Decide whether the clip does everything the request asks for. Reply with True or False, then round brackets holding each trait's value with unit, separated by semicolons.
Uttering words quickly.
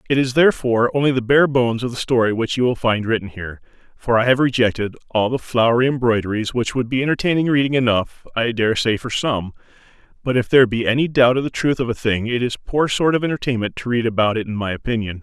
True (230 wpm)